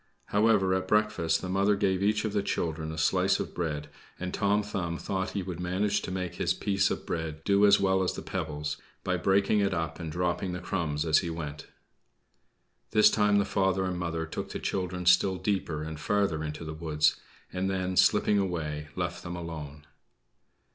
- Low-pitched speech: Yes, very low, 90 Hz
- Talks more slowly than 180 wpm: No, average, 195 wpm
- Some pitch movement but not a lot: Yes, average, 3.4 semitones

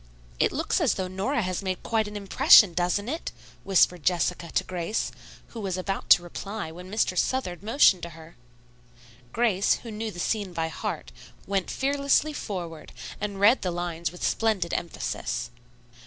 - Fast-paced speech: No, average, 160 wpm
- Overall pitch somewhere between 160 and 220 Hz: Yes, high, 190 Hz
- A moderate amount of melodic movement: Yes, average, 3.8 semitones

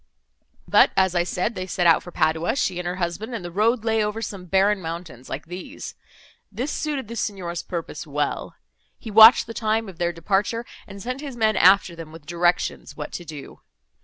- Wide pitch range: No, average, 4.3 semitones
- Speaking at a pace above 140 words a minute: Yes, average, 200 wpm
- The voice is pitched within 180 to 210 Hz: Yes, medium, 185 Hz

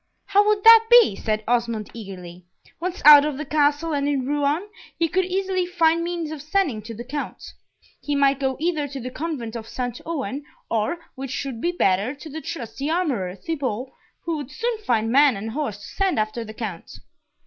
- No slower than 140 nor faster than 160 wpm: No, average, 195 wpm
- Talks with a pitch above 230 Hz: Yes, very high, 280 Hz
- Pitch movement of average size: No, wide, 6.1 semitones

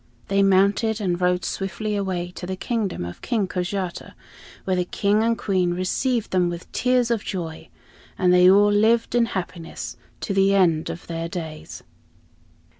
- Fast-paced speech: No, average, 165 wpm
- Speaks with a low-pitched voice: No, high, 190 Hz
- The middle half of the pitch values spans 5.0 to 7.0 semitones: No, average, 2.8 semitones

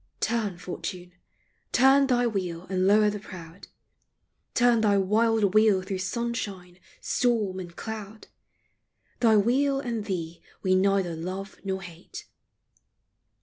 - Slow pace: Yes, slow, 120 wpm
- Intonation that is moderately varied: Yes, average, 3.5 semitones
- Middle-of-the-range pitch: No, high, 200 Hz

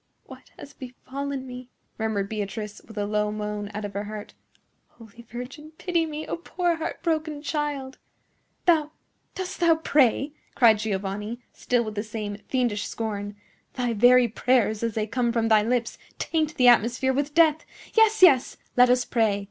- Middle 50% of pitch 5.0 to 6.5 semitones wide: Yes, wide, 5.5 semitones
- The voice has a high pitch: Yes, high, 245 Hz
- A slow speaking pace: No, average, 165 wpm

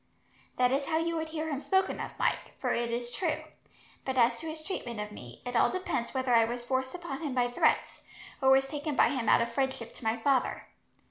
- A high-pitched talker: Yes, very high, 260 Hz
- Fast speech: Yes, fast, 230 wpm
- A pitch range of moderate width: Yes, average, 4.6 semitones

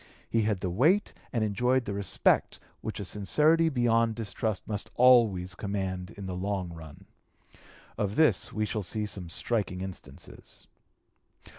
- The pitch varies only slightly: No, average, 3.7 semitones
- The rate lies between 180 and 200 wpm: No, average, 145 wpm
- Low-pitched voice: Yes, low, 105 Hz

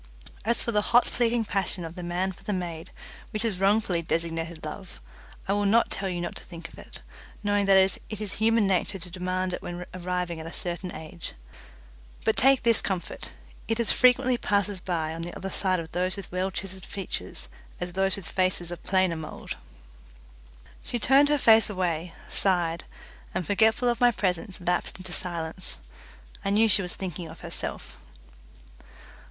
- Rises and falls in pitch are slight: No, average, 3.0 semitones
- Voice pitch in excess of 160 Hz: Yes, medium, 185 Hz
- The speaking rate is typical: Yes, average, 180 wpm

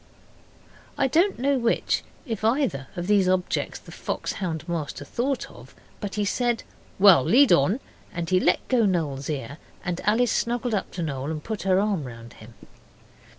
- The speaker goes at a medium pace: Yes, average, 175 wpm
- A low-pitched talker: No, high, 190 Hz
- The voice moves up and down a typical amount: No, wide, 6.9 semitones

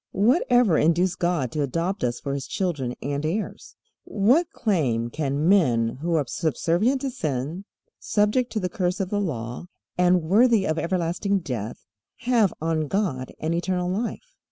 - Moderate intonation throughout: No, wide, 5.9 semitones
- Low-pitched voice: No, medium, 175 Hz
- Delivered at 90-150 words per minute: No, average, 160 wpm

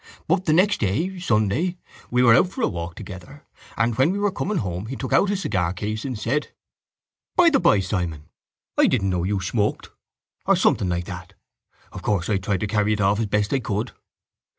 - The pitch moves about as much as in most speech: No, wide, 7.0 semitones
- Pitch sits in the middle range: No, low, 105 Hz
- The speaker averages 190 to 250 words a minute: Yes, average, 200 wpm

